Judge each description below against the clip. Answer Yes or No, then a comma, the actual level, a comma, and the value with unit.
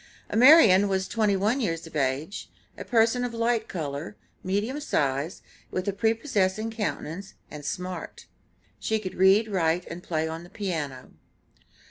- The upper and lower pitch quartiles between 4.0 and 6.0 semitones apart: Yes, average, 5.1 semitones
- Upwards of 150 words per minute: No, average, 145 wpm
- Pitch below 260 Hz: Yes, high, 190 Hz